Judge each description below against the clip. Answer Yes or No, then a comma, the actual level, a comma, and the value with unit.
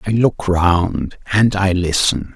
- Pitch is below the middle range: Yes, very low, 95 Hz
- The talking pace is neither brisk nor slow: Yes, average, 155 wpm